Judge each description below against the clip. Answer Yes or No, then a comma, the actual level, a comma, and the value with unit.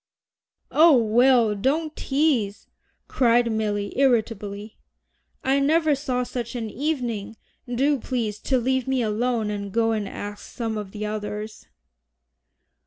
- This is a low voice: No, high, 235 Hz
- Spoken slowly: Yes, slow, 125 wpm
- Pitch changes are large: No, average, 3.8 semitones